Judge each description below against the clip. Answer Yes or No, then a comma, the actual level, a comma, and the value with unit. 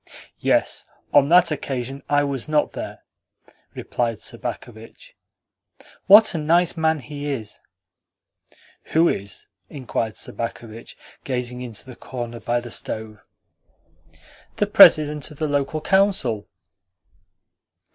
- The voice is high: No, low, 135 Hz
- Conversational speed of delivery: No, slow, 110 wpm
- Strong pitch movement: No, average, 4.6 semitones